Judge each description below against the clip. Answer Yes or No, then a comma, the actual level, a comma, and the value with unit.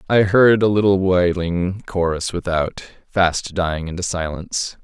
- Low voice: Yes, very low, 90 Hz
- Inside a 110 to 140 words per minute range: Yes, slow, 135 wpm